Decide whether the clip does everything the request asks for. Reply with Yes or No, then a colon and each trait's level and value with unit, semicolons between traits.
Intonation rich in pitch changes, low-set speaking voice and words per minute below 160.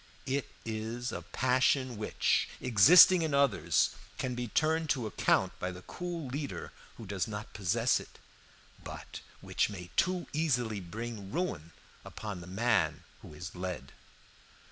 Yes: wide, 6.4 semitones; low, 115 Hz; average, 145 wpm